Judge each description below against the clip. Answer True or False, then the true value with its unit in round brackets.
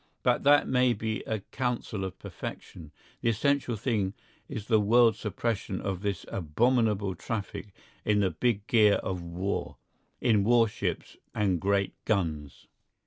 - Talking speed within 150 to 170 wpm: False (140 wpm)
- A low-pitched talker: True (105 Hz)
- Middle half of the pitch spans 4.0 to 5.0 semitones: False (3.4 semitones)